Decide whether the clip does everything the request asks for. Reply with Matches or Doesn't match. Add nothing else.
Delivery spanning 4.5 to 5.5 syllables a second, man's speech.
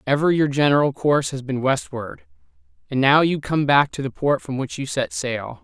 Matches